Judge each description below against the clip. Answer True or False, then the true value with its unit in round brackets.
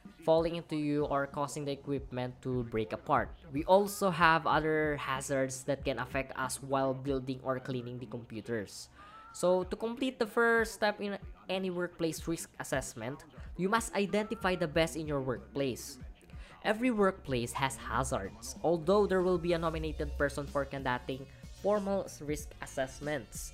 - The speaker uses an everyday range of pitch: False (5.9 semitones)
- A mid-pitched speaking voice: True (150 Hz)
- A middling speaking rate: True (155 wpm)